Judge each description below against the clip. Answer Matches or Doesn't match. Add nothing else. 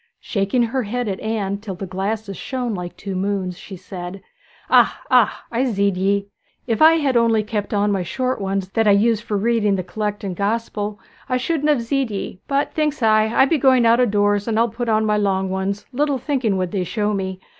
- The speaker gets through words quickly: Matches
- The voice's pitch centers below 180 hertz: Doesn't match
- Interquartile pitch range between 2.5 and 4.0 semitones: Matches